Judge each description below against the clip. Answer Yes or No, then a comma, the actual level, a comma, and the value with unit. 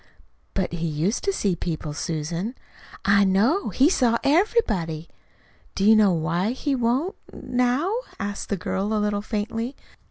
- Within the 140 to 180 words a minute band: Yes, average, 155 wpm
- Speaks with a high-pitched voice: Yes, high, 210 Hz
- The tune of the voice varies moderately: No, wide, 5.9 semitones